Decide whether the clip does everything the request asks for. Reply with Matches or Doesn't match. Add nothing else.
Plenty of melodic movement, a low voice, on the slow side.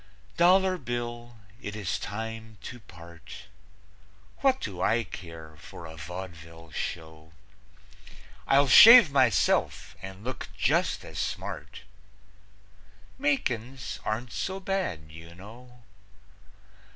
Matches